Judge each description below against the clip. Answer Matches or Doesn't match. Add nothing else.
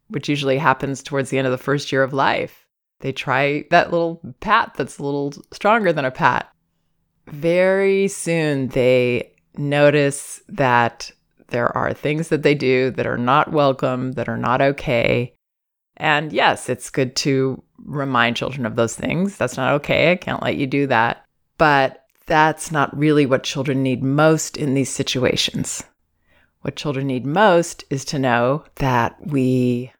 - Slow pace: Doesn't match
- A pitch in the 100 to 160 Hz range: Matches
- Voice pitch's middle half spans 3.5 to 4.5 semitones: Doesn't match